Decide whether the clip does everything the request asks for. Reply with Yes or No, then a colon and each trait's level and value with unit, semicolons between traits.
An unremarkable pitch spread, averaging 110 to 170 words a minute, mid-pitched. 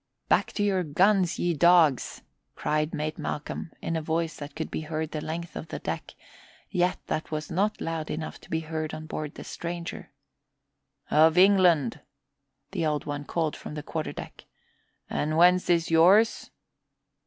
No: narrow, 2.2 semitones; average, 165 wpm; medium, 160 Hz